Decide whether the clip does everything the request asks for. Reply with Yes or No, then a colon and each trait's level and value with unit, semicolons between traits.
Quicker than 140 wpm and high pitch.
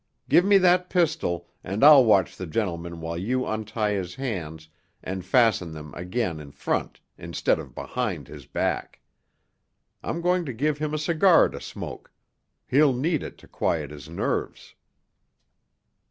No: average, 155 wpm; low, 110 Hz